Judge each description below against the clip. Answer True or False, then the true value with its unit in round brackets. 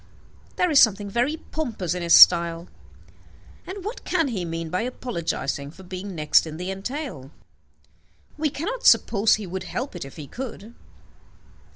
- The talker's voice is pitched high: True (195 Hz)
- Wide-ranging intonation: True (7.8 semitones)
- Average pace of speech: True (160 wpm)